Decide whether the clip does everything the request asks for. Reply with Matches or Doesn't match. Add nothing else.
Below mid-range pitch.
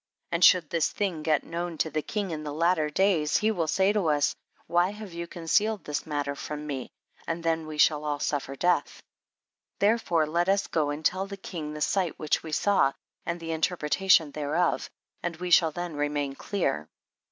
Doesn't match